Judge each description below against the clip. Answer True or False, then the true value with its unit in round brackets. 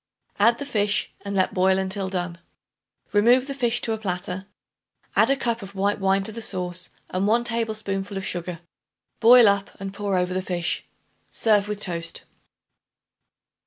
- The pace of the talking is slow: False (165 wpm)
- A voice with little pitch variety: False (3.0 semitones)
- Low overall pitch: False (200 Hz)